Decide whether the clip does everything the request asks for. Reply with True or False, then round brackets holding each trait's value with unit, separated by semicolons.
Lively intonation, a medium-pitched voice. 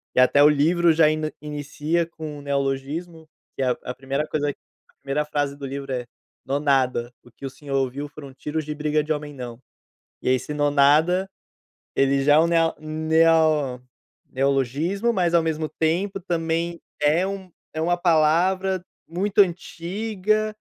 False (3.4 semitones; 155 Hz)